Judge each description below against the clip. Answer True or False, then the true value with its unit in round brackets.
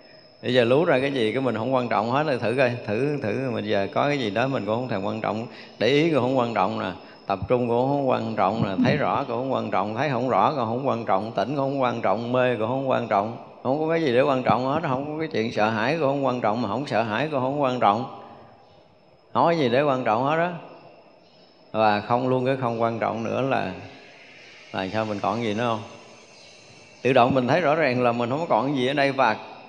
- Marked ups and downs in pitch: False (3.6 semitones)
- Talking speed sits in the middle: False (270 wpm)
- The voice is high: False (125 Hz)